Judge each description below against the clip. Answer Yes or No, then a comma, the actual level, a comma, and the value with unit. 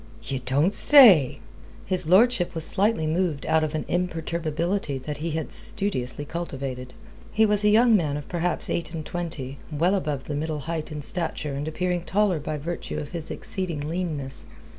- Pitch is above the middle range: No, medium, 160 Hz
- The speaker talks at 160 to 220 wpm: Yes, average, 175 wpm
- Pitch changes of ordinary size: Yes, average, 3.6 semitones